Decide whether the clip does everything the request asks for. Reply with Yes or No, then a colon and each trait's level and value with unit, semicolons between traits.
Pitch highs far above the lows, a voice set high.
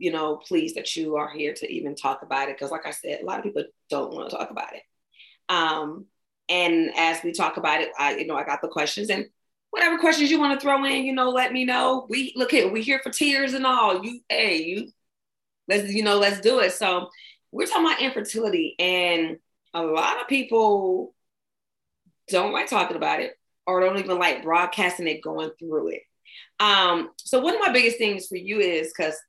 Yes: wide, 7.9 semitones; high, 200 Hz